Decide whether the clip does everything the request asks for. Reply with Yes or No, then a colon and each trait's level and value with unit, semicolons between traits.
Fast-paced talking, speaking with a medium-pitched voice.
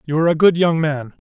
Yes: fast, 285 wpm; medium, 155 Hz